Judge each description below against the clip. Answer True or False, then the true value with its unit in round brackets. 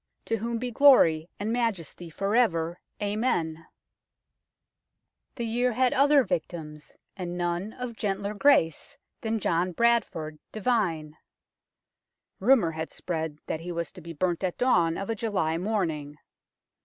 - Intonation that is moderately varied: False (5.8 semitones)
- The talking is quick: False (140 wpm)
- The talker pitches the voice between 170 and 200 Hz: True (190 Hz)